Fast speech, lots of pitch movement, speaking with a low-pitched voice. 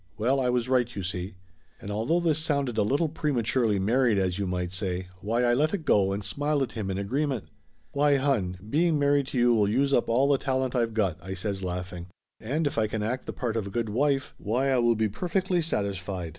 Yes: fast, 240 wpm; wide, 5.7 semitones; low, 120 Hz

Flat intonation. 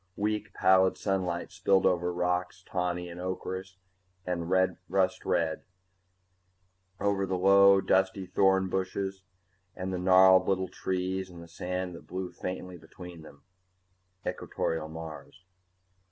Yes: narrow, 1.2 semitones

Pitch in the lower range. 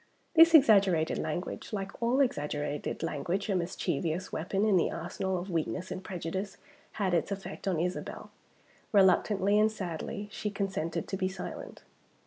No: high, 190 Hz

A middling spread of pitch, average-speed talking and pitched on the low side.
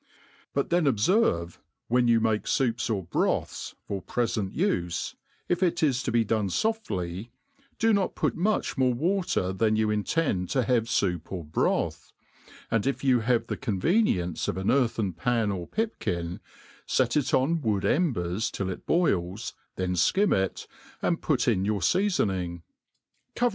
No: wide, 7.5 semitones; average, 160 wpm; low, 115 Hz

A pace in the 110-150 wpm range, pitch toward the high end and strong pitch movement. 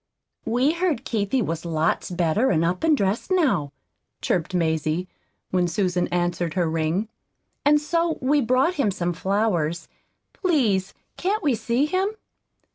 Yes: average, 140 wpm; high, 200 Hz; wide, 8.5 semitones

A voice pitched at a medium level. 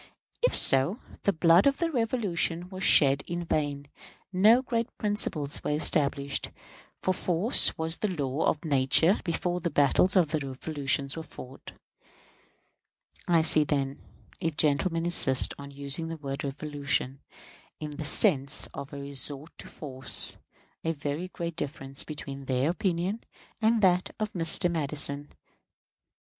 Yes: medium, 155 Hz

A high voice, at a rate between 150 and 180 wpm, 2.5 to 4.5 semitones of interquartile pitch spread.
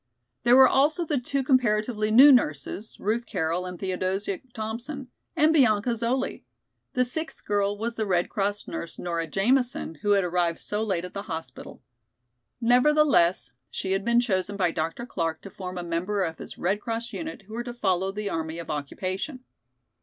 No: high, 205 Hz; average, 175 wpm; average, 5.1 semitones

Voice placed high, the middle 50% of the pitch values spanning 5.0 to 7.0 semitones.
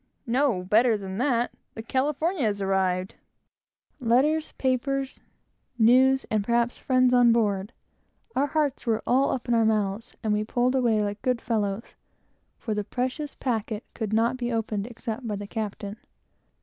No: high, 230 Hz; average, 3.4 semitones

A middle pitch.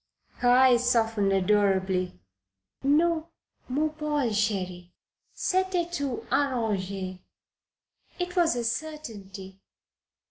No: high, 235 Hz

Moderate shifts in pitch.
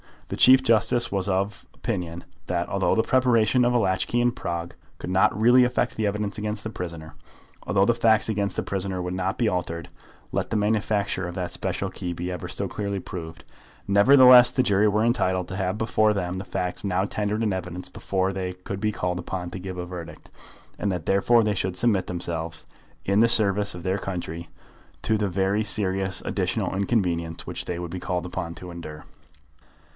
Yes: average, 3.0 semitones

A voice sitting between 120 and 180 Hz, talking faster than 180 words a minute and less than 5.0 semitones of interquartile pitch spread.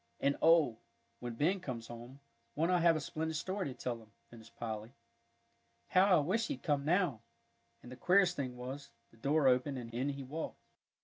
No: medium, 140 Hz; average, 190 wpm; wide, 5.4 semitones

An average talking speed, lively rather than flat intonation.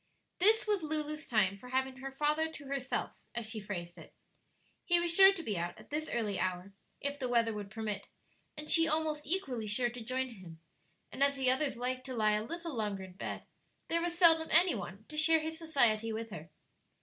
No: fast, 210 wpm; wide, 6.7 semitones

